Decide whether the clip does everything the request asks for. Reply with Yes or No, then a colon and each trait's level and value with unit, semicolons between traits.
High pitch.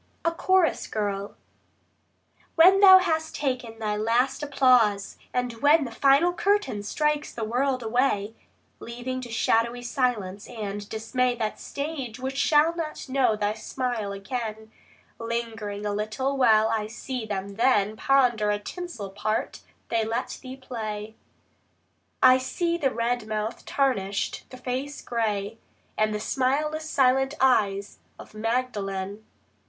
Yes: high, 240 Hz